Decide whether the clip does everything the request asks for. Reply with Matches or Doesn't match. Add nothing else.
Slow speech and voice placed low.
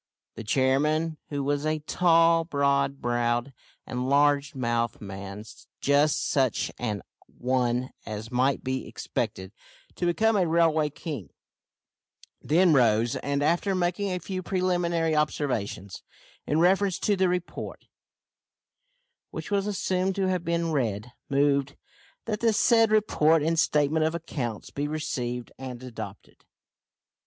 Doesn't match